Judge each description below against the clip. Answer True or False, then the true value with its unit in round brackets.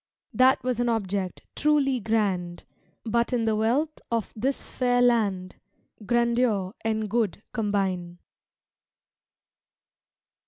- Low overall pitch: False (225 Hz)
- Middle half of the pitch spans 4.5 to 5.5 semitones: False (3.6 semitones)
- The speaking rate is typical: False (105 wpm)